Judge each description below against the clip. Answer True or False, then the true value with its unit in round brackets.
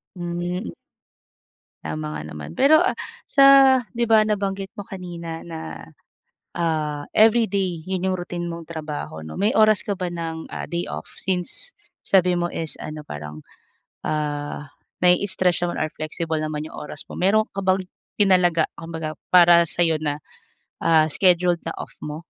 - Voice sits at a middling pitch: True (175 Hz)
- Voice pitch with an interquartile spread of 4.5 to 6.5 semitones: False (3.6 semitones)